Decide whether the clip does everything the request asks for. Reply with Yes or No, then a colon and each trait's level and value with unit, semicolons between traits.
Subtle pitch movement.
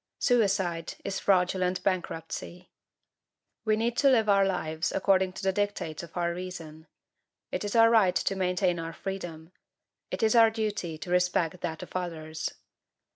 No: average, 3.2 semitones